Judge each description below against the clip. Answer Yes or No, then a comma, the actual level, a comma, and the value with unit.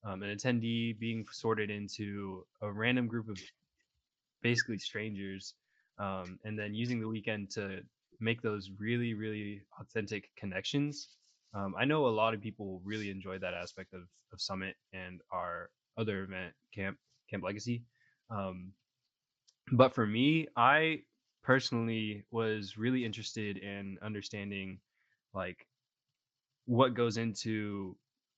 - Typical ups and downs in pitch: Yes, average, 3.3 semitones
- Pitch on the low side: Yes, low, 110 Hz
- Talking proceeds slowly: Yes, slow, 130 wpm